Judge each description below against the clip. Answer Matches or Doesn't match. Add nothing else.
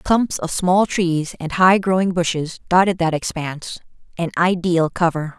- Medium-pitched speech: Matches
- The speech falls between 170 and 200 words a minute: Doesn't match